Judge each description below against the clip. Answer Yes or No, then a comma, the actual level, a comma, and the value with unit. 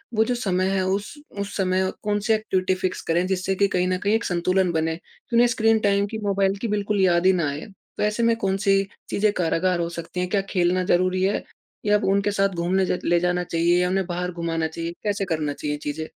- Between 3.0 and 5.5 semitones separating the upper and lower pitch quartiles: No, narrow, 2.5 semitones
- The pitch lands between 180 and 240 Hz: Yes, medium, 185 Hz